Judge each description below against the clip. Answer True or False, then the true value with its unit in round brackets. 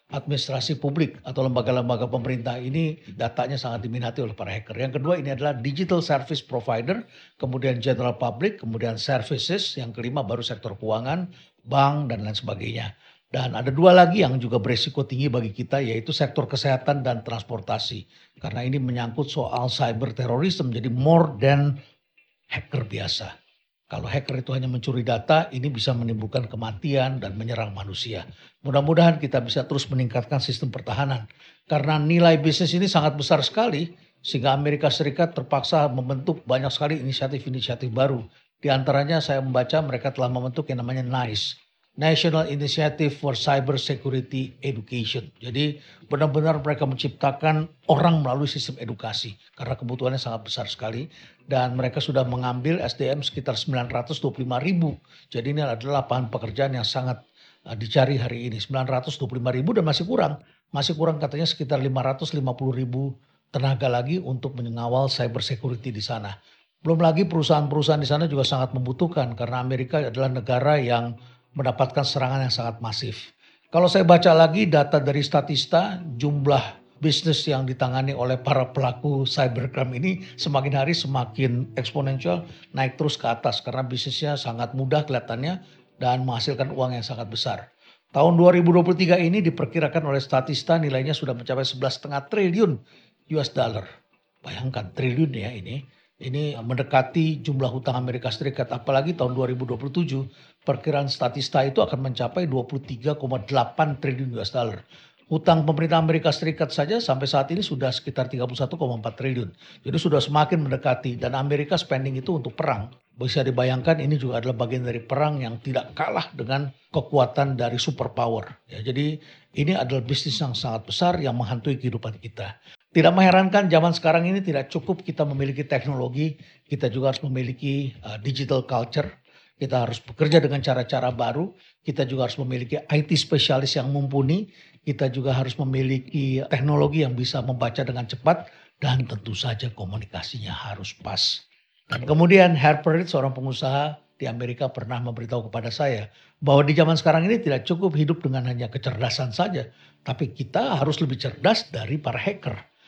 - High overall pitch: False (135 Hz)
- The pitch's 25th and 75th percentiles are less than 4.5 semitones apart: True (3.3 semitones)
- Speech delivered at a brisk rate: True (145 wpm)